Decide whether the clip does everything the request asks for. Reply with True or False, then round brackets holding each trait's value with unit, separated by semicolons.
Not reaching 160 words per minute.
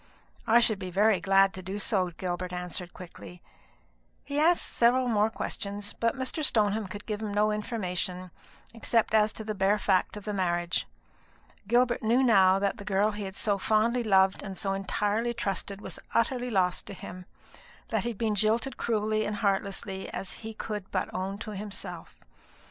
False (180 wpm)